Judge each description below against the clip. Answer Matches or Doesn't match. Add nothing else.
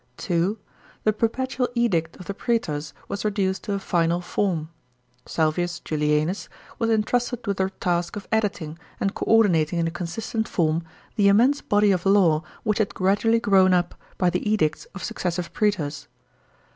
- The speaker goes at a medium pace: Matches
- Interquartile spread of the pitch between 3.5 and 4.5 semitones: Matches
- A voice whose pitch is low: Doesn't match